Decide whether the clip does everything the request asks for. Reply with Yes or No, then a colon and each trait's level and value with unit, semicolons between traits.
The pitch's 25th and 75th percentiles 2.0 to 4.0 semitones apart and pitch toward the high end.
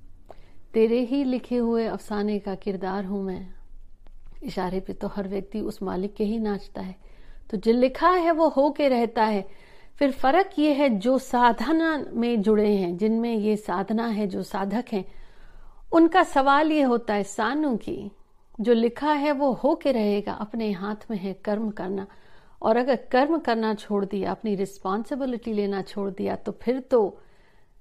No: average, 4.7 semitones; high, 220 Hz